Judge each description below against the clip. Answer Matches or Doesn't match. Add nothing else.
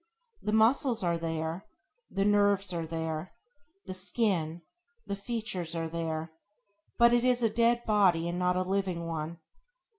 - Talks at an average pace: Matches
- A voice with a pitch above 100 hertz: Matches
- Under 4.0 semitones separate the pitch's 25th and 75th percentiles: Doesn't match